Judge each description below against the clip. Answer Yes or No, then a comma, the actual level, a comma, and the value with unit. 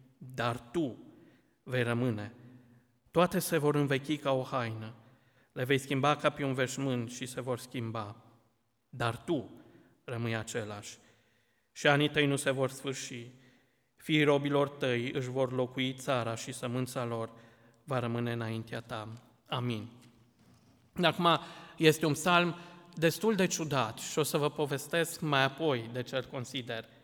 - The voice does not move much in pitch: No, average, 3.4 semitones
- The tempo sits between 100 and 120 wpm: No, average, 145 wpm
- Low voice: Yes, low, 130 Hz